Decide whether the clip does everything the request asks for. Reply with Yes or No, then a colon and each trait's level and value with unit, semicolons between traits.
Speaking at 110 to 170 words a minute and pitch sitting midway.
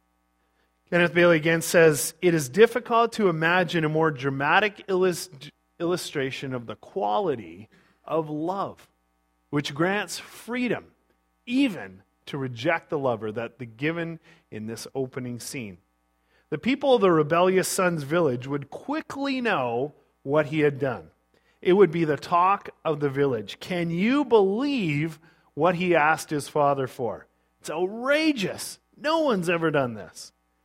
Yes: average, 140 wpm; medium, 160 Hz